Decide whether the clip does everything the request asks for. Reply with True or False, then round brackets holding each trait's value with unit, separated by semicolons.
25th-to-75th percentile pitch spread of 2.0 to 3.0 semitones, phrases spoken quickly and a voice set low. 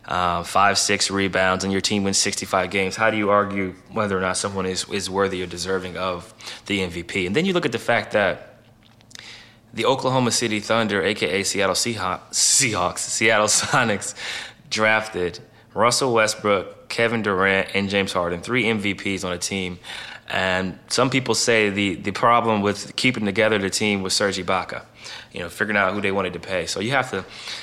False (2.7 semitones; 185 wpm; 100 Hz)